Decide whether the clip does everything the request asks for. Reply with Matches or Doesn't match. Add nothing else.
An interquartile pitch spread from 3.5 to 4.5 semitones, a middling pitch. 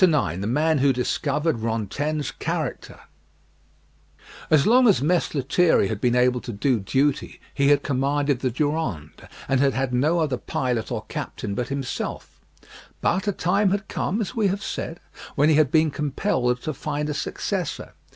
Matches